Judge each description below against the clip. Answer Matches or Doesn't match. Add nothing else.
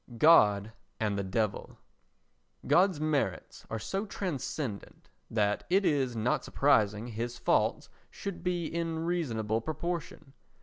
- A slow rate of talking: Matches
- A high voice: Doesn't match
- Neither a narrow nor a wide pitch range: Doesn't match